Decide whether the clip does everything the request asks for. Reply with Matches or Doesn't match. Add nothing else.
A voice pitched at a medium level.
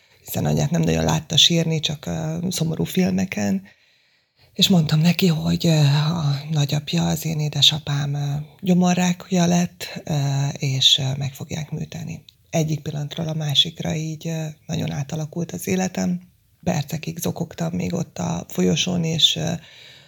Matches